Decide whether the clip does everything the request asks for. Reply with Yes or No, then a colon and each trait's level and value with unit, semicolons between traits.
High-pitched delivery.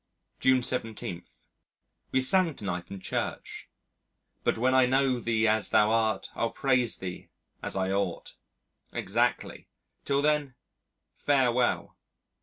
No: low, 120 Hz